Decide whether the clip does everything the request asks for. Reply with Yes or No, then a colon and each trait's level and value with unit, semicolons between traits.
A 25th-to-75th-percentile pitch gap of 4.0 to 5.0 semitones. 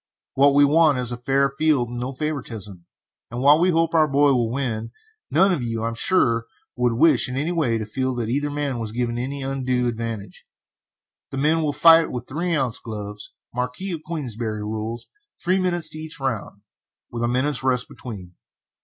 Yes: average, 4.3 semitones